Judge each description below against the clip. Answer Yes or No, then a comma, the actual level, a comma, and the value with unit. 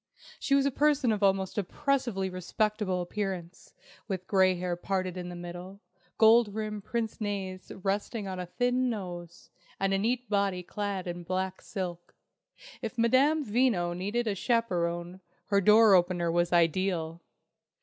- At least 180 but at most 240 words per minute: No, average, 150 wpm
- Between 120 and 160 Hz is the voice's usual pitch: No, high, 195 Hz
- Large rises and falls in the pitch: No, average, 3.7 semitones